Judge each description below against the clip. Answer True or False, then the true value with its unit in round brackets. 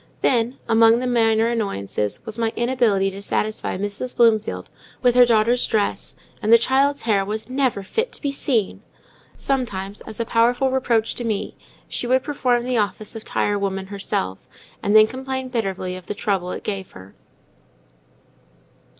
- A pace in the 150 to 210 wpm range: True (165 wpm)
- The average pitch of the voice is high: True (225 Hz)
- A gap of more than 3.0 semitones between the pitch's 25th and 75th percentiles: True (3.6 semitones)